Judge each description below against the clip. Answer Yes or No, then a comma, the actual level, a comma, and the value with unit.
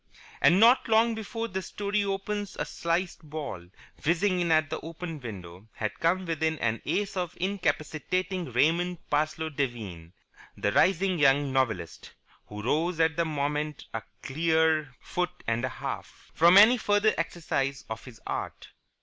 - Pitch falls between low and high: Yes, medium, 160 Hz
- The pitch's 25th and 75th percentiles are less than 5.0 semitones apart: No, average, 5.3 semitones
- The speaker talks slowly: No, average, 150 wpm